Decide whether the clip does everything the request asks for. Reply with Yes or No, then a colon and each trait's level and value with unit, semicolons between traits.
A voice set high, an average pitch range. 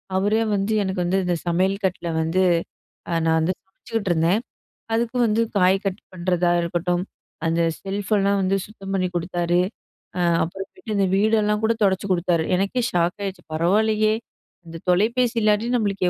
Yes: high, 195 Hz; average, 3.1 semitones